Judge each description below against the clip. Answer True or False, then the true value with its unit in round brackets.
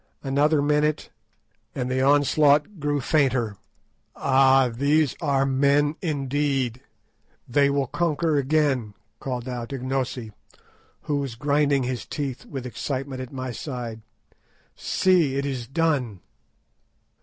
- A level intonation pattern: True (2.3 semitones)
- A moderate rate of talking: False (115 wpm)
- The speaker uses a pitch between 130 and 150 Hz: True (135 Hz)